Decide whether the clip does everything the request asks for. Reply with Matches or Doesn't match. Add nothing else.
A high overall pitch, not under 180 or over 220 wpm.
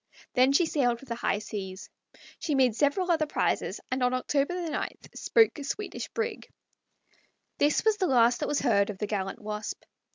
Matches